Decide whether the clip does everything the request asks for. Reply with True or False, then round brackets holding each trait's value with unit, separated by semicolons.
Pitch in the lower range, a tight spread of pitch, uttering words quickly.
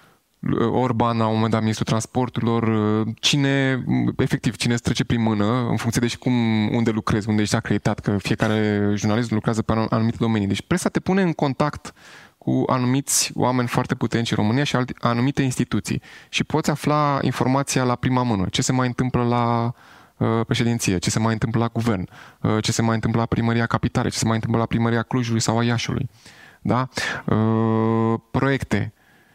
True (115 Hz; 2.3 semitones; 180 wpm)